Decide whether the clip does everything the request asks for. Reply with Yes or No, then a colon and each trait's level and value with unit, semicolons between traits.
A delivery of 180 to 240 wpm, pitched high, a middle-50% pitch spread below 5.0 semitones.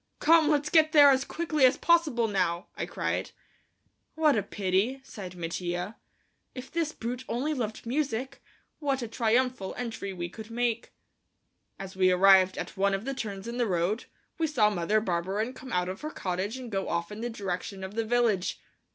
No: average, 185 wpm; high, 225 Hz; wide, 5.5 semitones